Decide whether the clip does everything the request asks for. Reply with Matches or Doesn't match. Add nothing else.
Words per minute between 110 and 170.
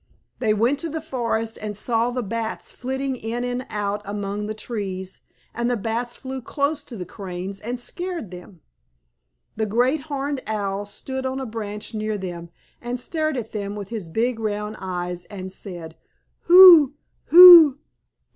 Matches